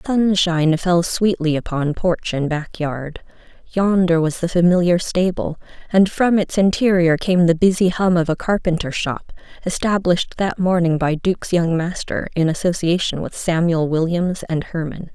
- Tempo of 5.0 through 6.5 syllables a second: No, 4.6 syllables/s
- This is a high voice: No, medium, 175 Hz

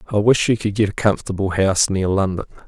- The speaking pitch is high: No, low, 100 Hz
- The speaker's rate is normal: No, fast, 225 wpm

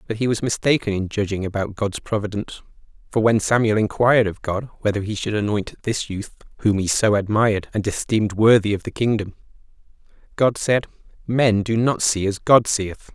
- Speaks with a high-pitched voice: No, low, 105 Hz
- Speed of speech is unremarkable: Yes, average, 185 wpm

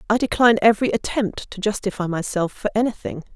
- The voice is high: Yes, high, 205 Hz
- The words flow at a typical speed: Yes, average, 160 wpm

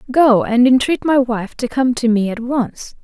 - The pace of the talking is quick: Yes, fast, 215 wpm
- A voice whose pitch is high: Yes, high, 245 Hz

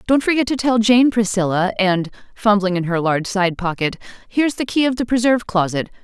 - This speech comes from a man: No, female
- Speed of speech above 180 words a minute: Yes, average, 200 wpm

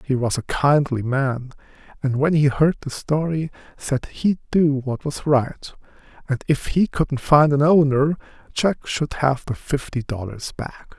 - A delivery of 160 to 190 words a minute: Yes, average, 170 wpm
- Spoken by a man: Yes, male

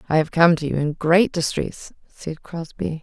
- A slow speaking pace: No, average, 200 wpm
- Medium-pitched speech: Yes, medium, 165 Hz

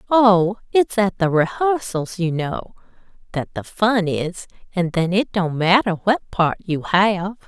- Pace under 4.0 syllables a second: Yes, 3.7 syllables/s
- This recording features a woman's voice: Yes, female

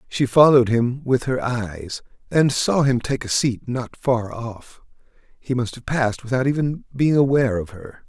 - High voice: No, low, 125 Hz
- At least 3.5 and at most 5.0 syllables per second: Yes, 4.6 syllables/s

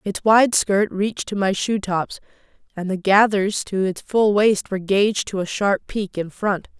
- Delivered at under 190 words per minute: No, average, 195 wpm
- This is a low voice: No, high, 200 Hz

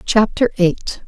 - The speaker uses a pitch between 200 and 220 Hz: Yes, high, 205 Hz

